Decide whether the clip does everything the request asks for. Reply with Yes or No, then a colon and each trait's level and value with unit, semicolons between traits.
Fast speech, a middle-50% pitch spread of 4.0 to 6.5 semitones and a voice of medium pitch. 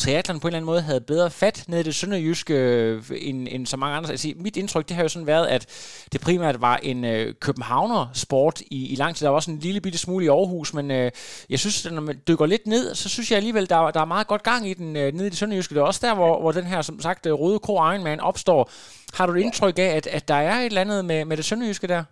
Yes: fast, 275 wpm; average, 4.6 semitones; medium, 165 Hz